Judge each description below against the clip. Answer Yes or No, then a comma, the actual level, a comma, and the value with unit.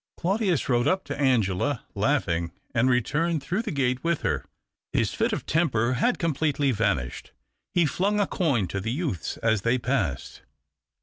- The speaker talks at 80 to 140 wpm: No, average, 165 wpm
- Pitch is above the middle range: No, low, 135 Hz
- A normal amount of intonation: No, wide, 6.6 semitones